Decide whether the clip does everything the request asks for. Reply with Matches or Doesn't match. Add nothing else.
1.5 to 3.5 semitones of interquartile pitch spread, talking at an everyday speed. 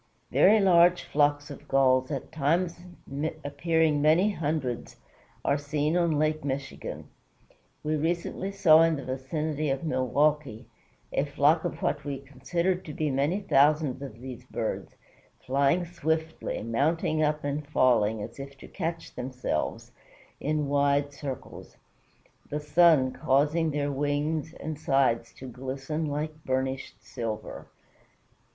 Doesn't match